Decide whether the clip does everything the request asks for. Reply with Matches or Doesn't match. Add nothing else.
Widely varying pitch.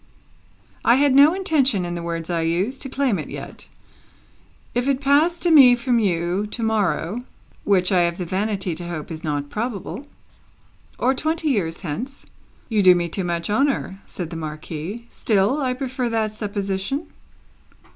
Matches